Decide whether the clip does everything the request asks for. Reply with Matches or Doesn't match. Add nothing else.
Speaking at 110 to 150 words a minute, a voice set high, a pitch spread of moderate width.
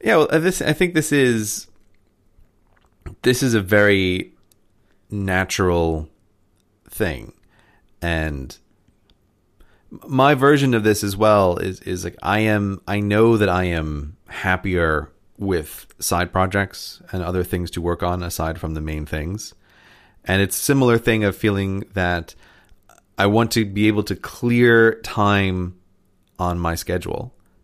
Doesn't match